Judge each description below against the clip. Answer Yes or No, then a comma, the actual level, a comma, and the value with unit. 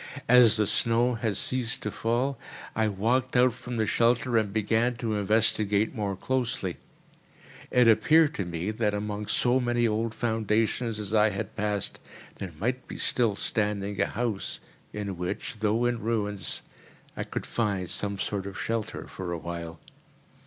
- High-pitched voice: No, low, 110 Hz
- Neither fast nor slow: Yes, average, 160 wpm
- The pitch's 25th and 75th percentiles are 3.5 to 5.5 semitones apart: No, average, 2.7 semitones